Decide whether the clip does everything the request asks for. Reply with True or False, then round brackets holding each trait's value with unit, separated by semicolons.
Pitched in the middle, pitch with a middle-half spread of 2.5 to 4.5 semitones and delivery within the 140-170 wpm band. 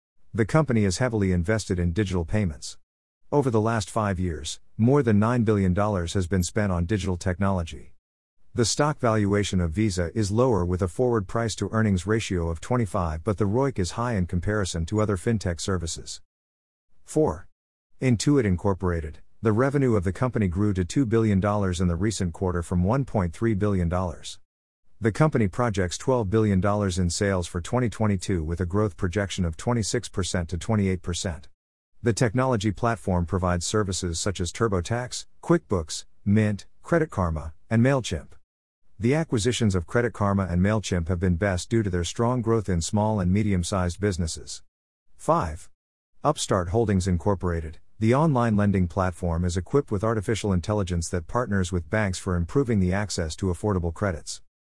False (100 Hz; 3.9 semitones; 160 wpm)